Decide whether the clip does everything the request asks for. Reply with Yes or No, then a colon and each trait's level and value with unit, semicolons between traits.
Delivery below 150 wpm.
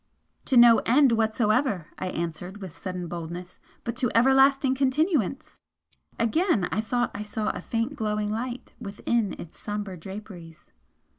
Yes: average, 140 wpm